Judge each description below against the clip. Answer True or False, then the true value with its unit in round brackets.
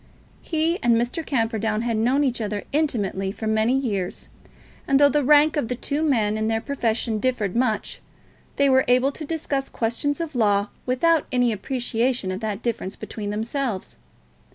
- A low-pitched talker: False (240 Hz)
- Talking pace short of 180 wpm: True (170 wpm)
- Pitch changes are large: False (4.3 semitones)